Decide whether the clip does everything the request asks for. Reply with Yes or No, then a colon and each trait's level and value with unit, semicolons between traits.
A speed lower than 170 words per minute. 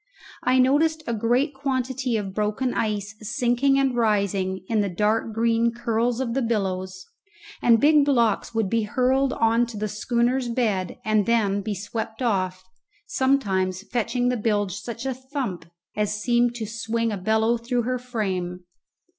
Yes: average, 160 wpm